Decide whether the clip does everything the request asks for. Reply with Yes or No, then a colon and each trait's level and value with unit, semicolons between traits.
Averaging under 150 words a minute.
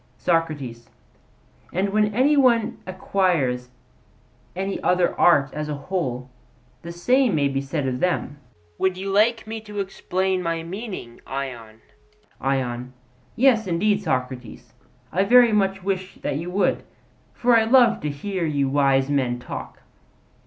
Yes: average, 140 wpm